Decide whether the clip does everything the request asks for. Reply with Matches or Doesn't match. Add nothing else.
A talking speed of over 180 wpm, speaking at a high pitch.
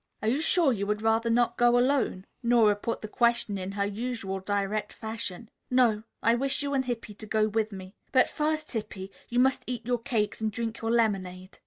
Matches